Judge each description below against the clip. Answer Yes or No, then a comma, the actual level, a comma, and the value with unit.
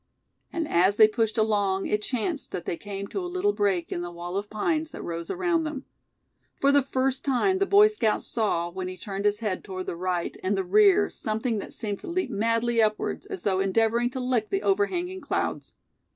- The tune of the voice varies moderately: No, wide, 7.2 semitones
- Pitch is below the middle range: No, high, 220 Hz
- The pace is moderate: No, fast, 210 wpm